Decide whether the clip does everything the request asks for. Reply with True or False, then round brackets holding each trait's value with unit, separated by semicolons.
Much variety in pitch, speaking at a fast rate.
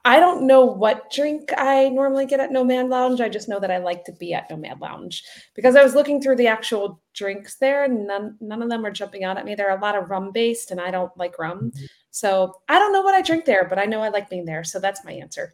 True (5.8 semitones; 285 wpm)